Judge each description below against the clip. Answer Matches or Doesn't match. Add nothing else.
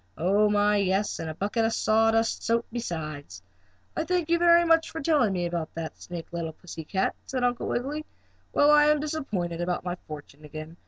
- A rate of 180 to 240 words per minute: Matches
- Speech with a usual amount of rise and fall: Doesn't match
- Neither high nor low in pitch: Doesn't match